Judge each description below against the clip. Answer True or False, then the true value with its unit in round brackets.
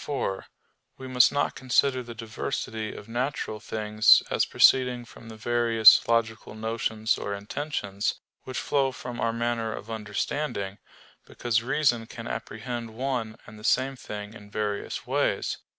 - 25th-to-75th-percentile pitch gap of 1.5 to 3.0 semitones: True (2.7 semitones)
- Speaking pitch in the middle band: False (115 Hz)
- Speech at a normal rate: True (145 wpm)